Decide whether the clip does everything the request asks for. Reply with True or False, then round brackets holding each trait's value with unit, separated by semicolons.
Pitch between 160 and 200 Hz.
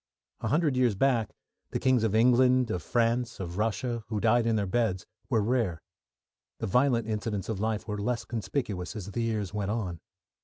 False (115 Hz)